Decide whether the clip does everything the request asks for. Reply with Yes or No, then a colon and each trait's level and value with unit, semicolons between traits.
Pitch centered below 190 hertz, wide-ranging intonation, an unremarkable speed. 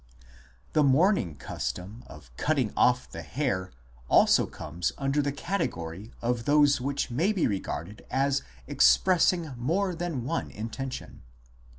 No: low, 135 Hz; wide, 6.6 semitones; slow, 125 wpm